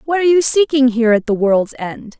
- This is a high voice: Yes, very high, 255 Hz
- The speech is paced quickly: Yes, fast, 245 wpm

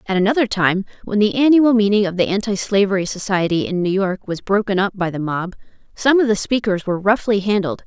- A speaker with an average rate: No, fast, 215 wpm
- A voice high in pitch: Yes, high, 200 Hz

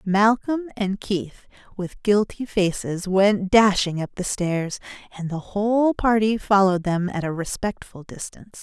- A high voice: Yes, high, 195 Hz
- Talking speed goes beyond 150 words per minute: No, average, 145 wpm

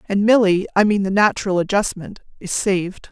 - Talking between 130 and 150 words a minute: Yes, slow, 135 wpm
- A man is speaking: No, female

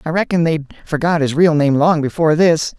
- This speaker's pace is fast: Yes, fast, 215 wpm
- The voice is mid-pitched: Yes, medium, 160 Hz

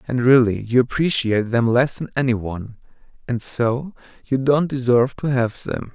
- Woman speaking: No, male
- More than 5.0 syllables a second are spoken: No, 4.9 syllables/s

